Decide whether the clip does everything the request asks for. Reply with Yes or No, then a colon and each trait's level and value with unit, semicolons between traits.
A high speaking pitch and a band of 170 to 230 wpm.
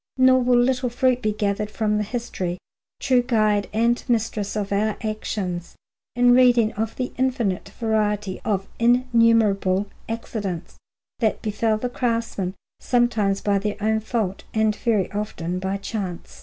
No: high, 215 Hz; average, 140 wpm